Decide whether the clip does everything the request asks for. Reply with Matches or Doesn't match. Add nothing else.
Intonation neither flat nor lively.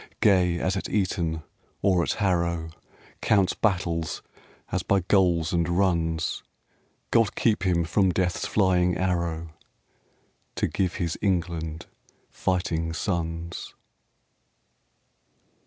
Doesn't match